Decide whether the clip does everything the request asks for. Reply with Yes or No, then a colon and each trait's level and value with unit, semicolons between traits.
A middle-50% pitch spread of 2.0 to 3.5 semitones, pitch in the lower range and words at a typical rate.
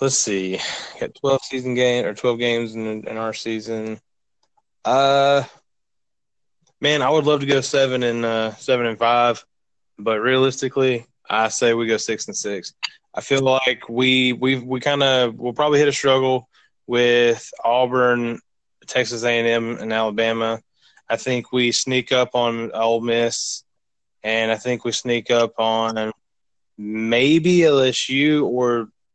Yes: narrow, 2.5 semitones; low, 120 Hz; average, 155 wpm